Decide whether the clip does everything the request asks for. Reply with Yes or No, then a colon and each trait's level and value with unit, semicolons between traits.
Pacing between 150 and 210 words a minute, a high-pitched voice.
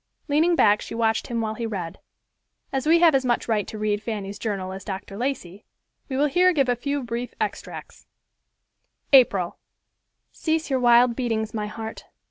Yes: average, 170 wpm; high, 230 Hz